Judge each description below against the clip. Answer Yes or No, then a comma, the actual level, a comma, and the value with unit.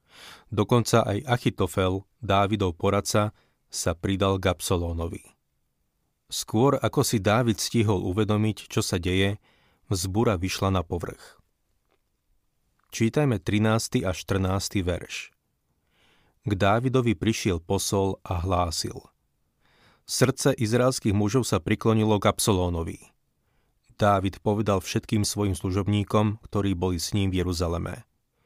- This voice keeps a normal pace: No, slow, 105 wpm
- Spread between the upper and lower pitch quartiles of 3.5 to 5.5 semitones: No, average, 3.0 semitones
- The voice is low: Yes, low, 100 Hz